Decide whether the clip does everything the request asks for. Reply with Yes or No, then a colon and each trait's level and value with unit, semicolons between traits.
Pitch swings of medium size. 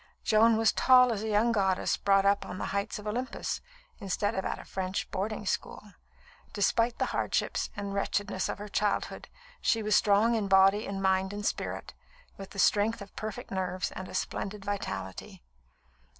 No: narrow, 1.8 semitones